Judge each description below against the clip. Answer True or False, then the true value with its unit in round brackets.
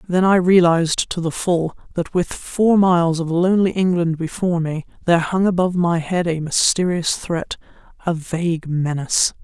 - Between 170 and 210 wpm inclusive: False (160 wpm)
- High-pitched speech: False (170 Hz)